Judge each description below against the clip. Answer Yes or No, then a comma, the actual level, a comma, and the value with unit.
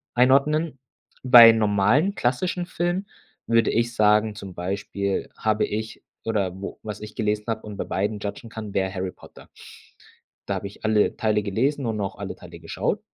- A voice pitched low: Yes, low, 110 Hz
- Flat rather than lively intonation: No, average, 3.2 semitones